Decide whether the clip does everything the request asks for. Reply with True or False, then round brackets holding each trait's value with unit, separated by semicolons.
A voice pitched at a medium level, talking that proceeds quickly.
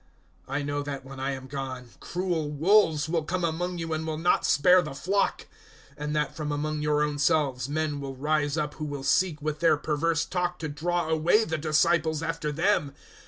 True (155 Hz; 210 wpm)